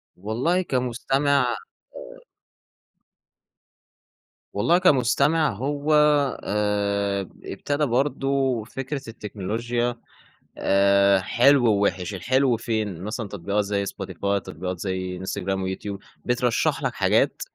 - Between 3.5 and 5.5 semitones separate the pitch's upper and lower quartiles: Yes, average, 5.0 semitones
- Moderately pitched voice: No, low, 110 Hz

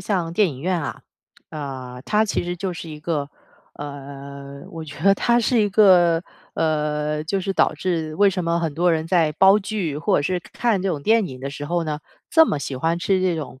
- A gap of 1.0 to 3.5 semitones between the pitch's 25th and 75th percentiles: No, average, 4.3 semitones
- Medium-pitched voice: Yes, medium, 165 Hz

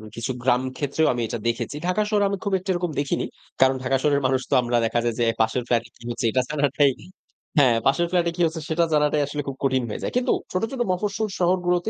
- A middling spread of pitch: No, wide, 5.7 semitones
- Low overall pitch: No, medium, 145 Hz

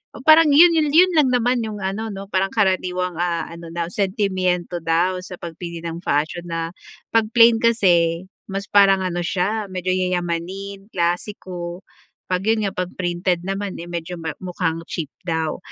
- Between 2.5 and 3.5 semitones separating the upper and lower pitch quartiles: Yes, average, 2.8 semitones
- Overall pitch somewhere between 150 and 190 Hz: Yes, medium, 185 Hz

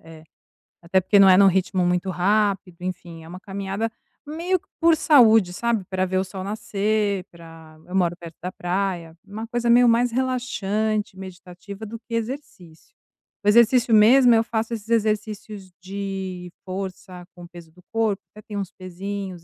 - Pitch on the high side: Yes, high, 195 Hz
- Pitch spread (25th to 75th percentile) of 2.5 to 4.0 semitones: Yes, average, 3.4 semitones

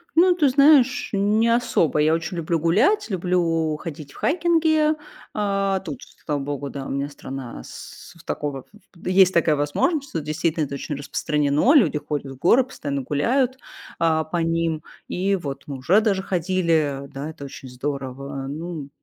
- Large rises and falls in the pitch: Yes, wide, 5.7 semitones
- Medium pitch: Yes, medium, 165 Hz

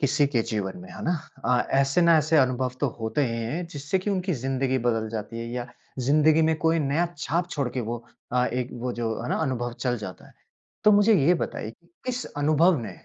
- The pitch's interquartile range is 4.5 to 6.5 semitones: Yes, average, 5.1 semitones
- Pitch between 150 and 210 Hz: No, low, 135 Hz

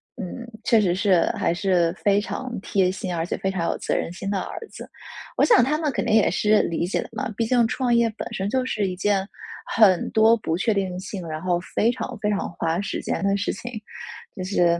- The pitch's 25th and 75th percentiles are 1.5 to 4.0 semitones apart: Yes, average, 3.6 semitones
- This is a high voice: Yes, high, 195 Hz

